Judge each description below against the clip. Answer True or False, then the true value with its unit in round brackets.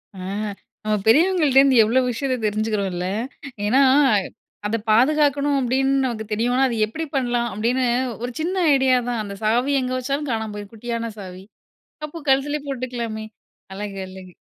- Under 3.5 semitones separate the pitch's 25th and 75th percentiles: False (3.8 semitones)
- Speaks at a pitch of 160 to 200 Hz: False (245 Hz)